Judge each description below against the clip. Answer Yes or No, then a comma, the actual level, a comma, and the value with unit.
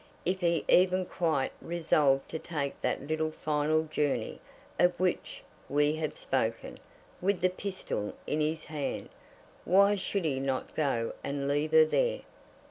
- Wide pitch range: No, average, 3.8 semitones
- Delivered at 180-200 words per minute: No, average, 145 wpm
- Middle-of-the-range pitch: Yes, medium, 155 Hz